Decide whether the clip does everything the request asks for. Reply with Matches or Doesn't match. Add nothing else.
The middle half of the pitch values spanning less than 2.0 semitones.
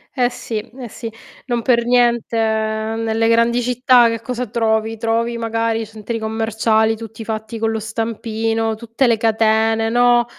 Matches